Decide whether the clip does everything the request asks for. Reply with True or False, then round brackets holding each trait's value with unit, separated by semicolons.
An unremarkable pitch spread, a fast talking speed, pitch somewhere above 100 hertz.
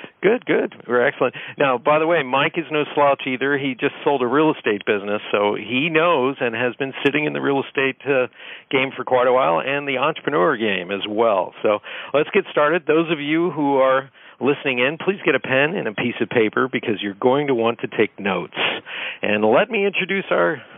True (3.4 semitones; 220 wpm; 135 Hz)